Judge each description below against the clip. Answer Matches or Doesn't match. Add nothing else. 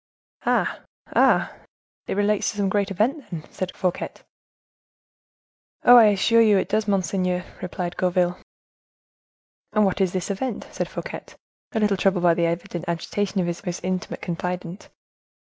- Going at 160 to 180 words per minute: Doesn't match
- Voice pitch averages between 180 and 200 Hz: Matches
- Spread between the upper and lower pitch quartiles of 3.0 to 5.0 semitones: Doesn't match